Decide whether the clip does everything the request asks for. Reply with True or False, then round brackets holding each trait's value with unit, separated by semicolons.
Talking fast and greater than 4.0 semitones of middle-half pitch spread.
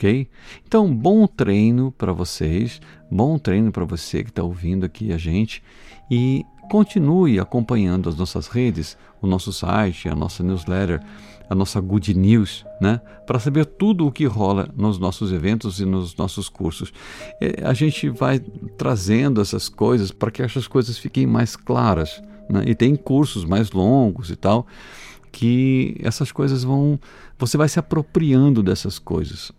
False (155 wpm; 5.6 semitones)